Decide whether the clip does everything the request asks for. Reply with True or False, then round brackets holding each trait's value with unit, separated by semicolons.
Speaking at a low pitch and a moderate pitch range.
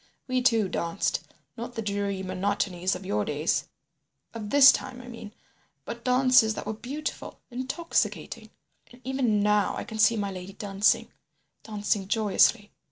False (215 Hz; 3.7 semitones)